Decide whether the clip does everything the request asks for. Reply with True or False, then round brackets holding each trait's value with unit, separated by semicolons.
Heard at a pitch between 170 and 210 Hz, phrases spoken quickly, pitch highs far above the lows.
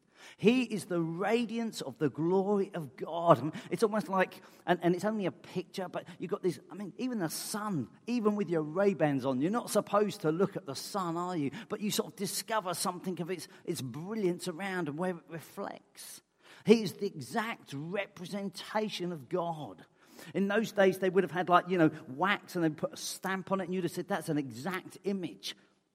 False (185 Hz; 215 wpm; 3.1 semitones)